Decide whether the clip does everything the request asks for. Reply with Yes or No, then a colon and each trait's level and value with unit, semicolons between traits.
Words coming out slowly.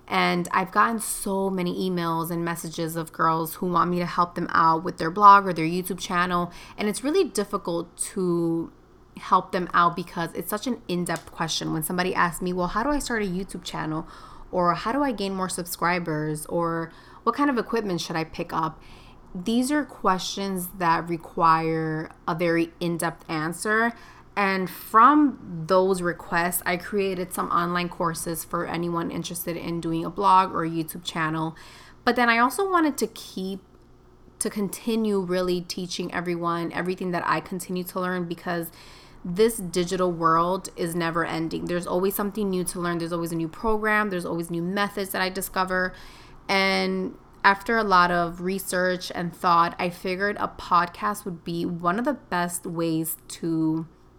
No: average, 175 wpm